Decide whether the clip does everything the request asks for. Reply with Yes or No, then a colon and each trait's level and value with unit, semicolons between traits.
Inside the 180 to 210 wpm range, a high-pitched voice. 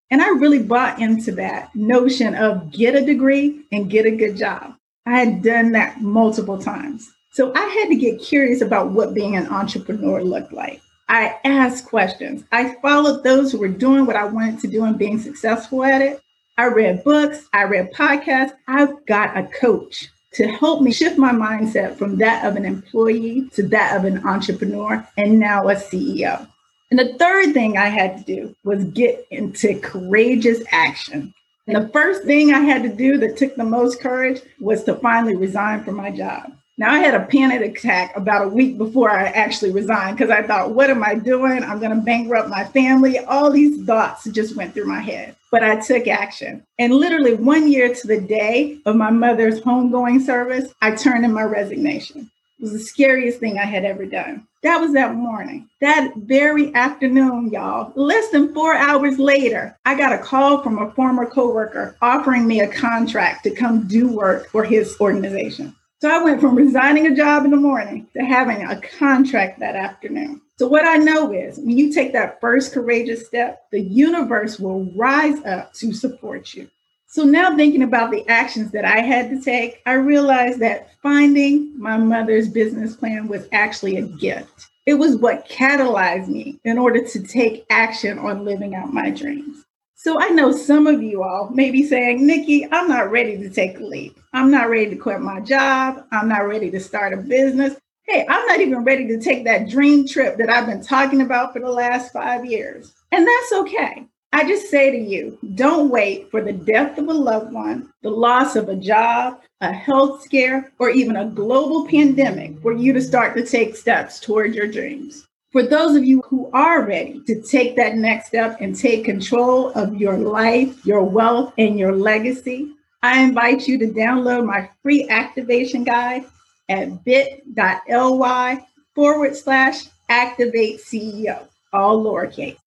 Yes: average, 190 wpm; high, 245 Hz